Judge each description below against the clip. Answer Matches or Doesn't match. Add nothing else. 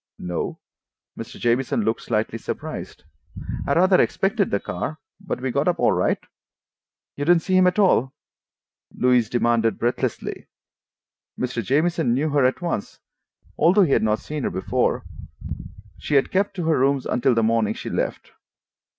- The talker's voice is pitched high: Doesn't match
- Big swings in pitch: Matches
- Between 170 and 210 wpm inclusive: Doesn't match